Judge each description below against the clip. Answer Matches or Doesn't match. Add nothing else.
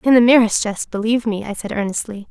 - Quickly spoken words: Matches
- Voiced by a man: Doesn't match